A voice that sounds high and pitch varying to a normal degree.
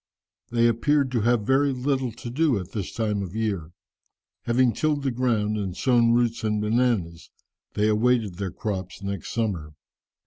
No: low, 115 Hz; average, 3.6 semitones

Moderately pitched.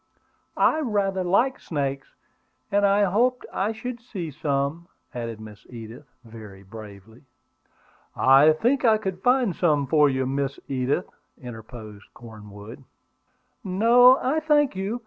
Yes: medium, 150 Hz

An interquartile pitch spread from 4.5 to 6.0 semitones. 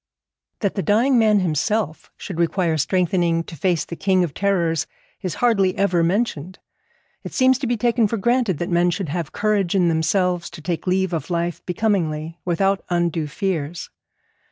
No: average, 3.2 semitones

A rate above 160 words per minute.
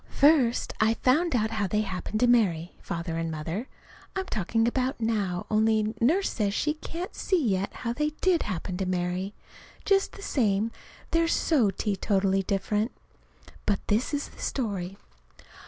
No: average, 155 wpm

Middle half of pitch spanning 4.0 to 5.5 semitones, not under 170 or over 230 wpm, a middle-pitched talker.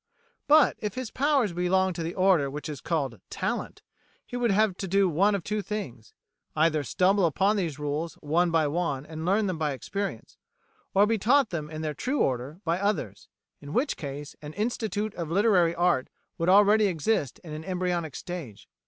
Yes: average, 5.0 semitones; average, 190 wpm; medium, 175 Hz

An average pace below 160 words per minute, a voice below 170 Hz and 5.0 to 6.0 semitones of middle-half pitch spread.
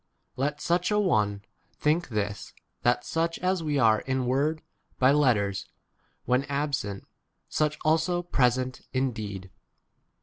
Yes: slow, 135 wpm; low, 135 Hz; wide, 5.5 semitones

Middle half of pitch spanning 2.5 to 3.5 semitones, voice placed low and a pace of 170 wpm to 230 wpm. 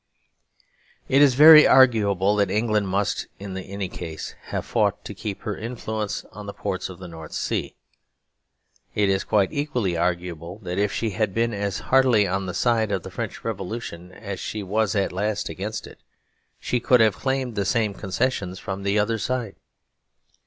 Yes: average, 3.0 semitones; low, 100 Hz; average, 175 wpm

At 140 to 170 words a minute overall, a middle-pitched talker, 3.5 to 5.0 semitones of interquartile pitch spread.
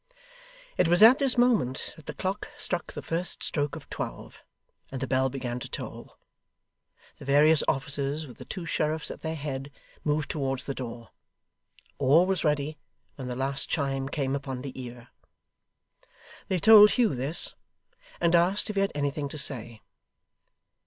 Yes: average, 165 wpm; medium, 145 Hz; average, 4.1 semitones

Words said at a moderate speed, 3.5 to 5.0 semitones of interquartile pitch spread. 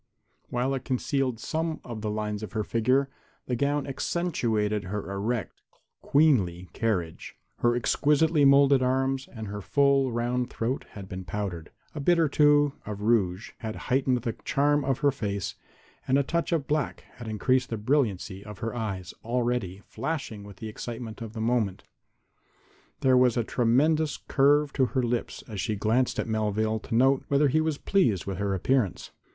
Yes: average, 170 wpm; average, 4.6 semitones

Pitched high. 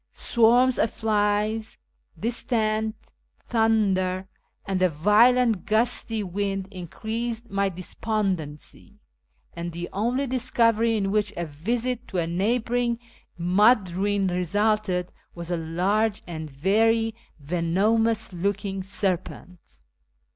Yes: high, 205 Hz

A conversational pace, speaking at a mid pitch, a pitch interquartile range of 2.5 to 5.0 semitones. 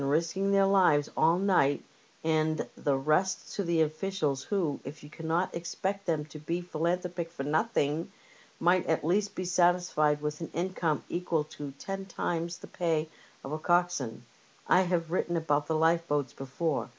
Yes: average, 160 wpm; medium, 165 Hz; average, 3.0 semitones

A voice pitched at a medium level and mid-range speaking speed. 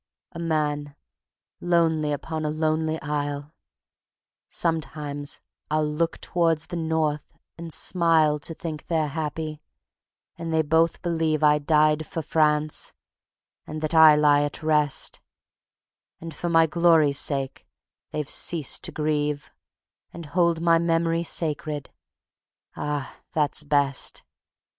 No: medium, 155 Hz; slow, 120 wpm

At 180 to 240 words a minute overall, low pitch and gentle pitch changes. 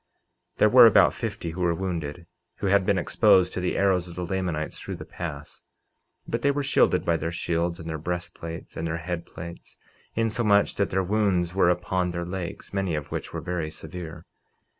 Yes: average, 200 wpm; very low, 90 Hz; narrow, 2.3 semitones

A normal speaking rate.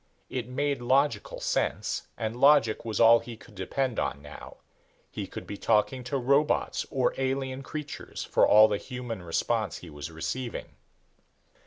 Yes: average, 155 wpm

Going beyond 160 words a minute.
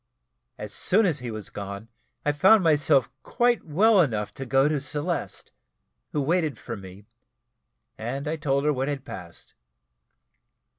No: average, 150 wpm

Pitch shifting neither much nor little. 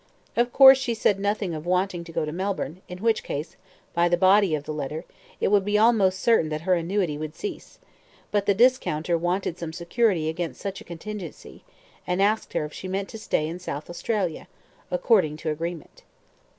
Yes: average, 4.2 semitones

